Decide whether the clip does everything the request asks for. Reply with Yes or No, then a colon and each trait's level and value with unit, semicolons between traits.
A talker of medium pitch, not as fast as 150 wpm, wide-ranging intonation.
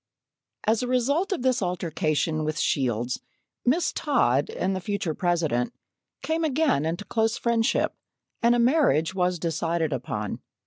Yes: medium, 180 Hz; average, 140 wpm; wide, 7.8 semitones